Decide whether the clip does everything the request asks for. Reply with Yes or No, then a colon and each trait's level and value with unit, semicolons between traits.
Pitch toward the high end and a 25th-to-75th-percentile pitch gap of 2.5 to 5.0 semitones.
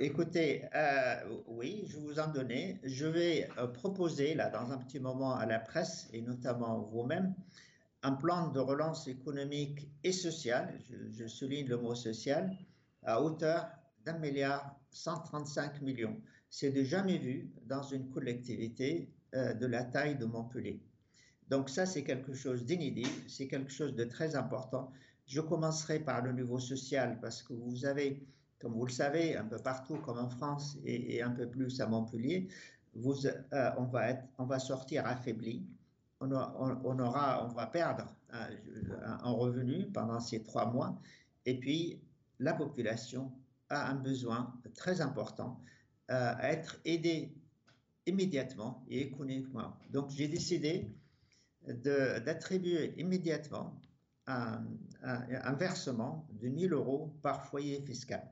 No: low, 135 Hz; average, 3.4 semitones